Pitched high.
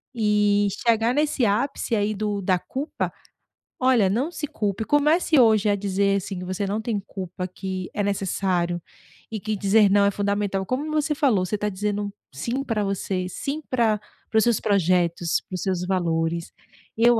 Yes: high, 205 Hz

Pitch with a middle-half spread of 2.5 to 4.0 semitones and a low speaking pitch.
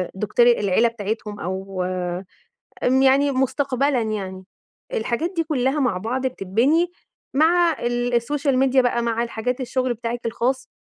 No: average, 3.3 semitones; high, 245 Hz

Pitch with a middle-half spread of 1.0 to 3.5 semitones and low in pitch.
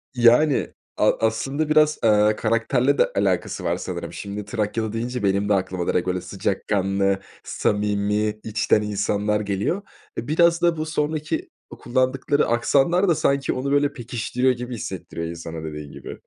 No: wide, 5.5 semitones; low, 110 Hz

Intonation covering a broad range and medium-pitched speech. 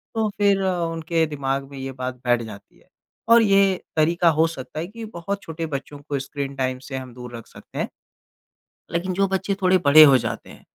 Yes: wide, 5.7 semitones; medium, 155 Hz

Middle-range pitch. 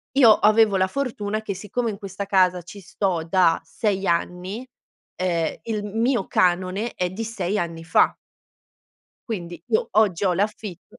No: high, 195 Hz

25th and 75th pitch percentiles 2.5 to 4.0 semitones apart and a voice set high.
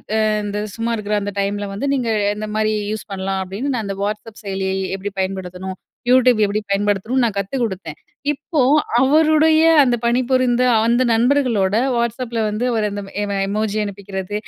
Yes: average, 3.7 semitones; high, 215 Hz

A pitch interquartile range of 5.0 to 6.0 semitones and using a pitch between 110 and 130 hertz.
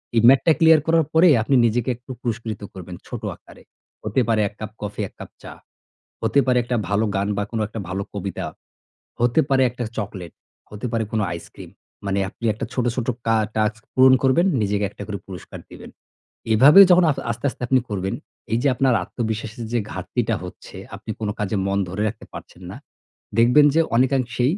No: average, 3.6 semitones; low, 115 Hz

